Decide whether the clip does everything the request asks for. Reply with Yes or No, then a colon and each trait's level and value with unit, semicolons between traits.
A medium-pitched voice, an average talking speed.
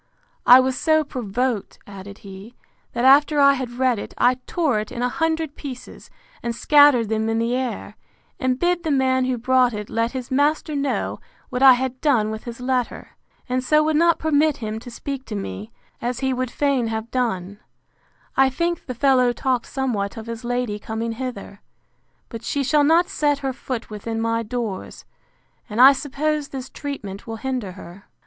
No: very high, 250 Hz; average, 185 wpm